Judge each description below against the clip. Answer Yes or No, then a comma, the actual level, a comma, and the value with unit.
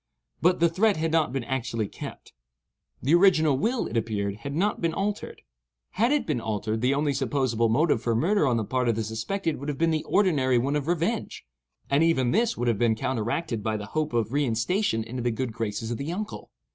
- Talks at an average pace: No, fast, 215 wpm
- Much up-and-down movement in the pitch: Yes, wide, 6.4 semitones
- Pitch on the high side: No, low, 135 Hz